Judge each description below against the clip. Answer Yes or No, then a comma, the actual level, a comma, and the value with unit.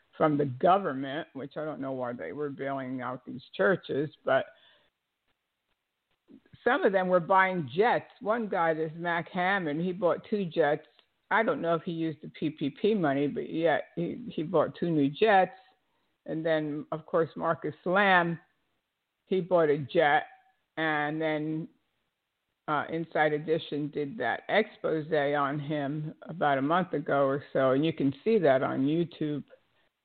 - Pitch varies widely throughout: No, average, 3.8 semitones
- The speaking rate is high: No, average, 160 wpm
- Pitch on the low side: No, medium, 160 Hz